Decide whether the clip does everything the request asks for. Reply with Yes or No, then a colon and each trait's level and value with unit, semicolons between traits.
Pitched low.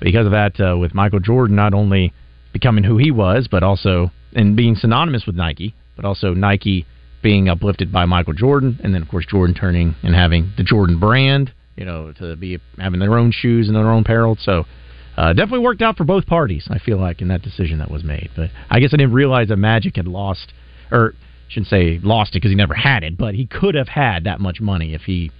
Yes: low, 100 Hz